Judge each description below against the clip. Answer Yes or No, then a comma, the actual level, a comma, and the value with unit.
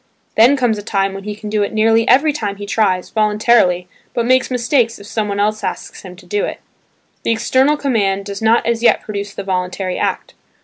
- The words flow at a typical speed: No, fast, 210 wpm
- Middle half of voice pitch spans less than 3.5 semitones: Yes, average, 2.7 semitones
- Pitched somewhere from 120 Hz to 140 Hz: No, high, 215 Hz